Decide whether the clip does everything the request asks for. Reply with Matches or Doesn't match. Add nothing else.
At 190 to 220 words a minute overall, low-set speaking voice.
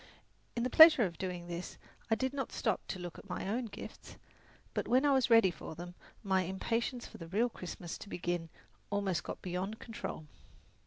Doesn't match